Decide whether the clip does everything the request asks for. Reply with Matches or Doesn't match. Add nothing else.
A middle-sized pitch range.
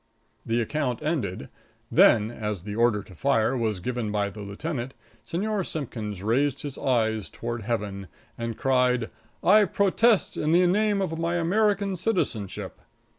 Doesn't match